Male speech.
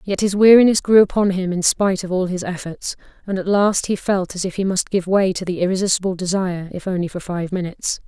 No: female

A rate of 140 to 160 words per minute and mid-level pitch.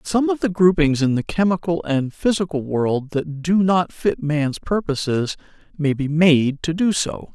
No: average, 180 wpm; medium, 160 Hz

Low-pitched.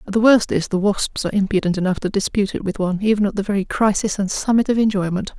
No: high, 200 Hz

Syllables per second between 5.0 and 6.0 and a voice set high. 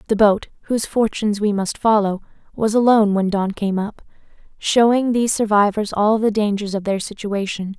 Yes: 5.3 syllables/s; high, 210 Hz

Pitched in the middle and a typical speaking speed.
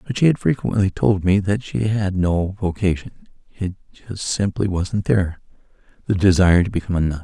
No: very low, 95 Hz; average, 175 wpm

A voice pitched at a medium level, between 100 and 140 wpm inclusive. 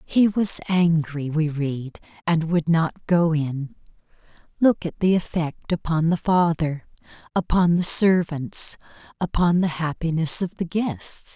Yes: medium, 165 Hz; slow, 135 wpm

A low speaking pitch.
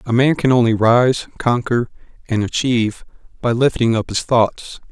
Yes: low, 120 Hz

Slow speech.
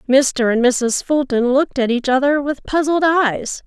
No: average, 180 wpm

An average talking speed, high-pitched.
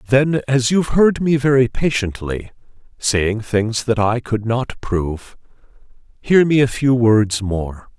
No: average, 150 wpm; low, 120 Hz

